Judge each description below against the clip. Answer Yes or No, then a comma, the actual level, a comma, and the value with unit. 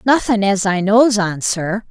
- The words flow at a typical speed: Yes, average, 190 wpm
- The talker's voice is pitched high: Yes, high, 205 Hz